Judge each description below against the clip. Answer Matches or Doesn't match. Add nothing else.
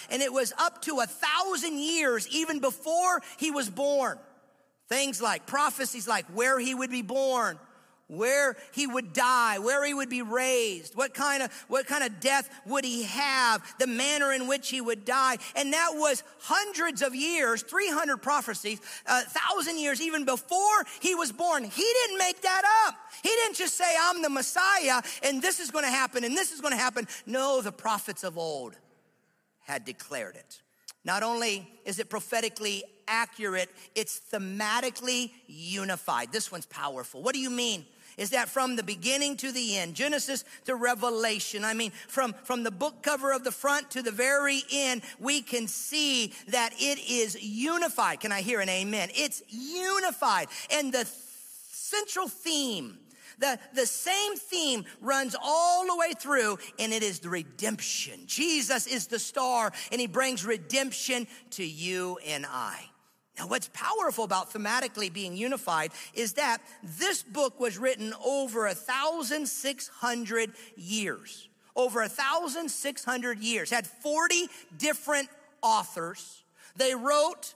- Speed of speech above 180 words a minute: Doesn't match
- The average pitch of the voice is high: Matches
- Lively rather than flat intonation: Doesn't match